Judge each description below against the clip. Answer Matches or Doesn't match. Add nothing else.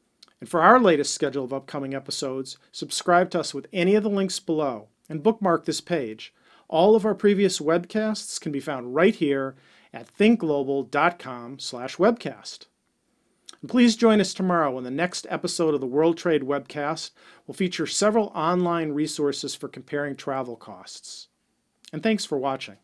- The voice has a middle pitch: Matches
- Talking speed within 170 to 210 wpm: Doesn't match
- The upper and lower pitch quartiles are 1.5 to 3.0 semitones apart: Doesn't match